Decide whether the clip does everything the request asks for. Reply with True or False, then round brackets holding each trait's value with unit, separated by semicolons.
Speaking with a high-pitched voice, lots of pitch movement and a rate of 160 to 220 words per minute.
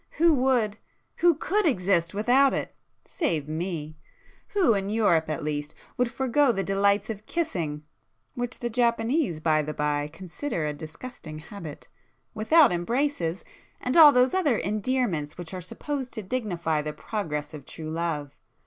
False (200 Hz; 8.1 semitones; 140 wpm)